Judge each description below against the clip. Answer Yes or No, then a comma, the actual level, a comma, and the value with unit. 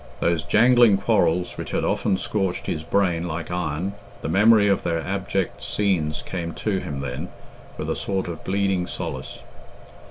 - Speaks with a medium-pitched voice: No, very low, 90 Hz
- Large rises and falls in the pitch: No, average, 3.1 semitones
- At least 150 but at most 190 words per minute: Yes, average, 160 wpm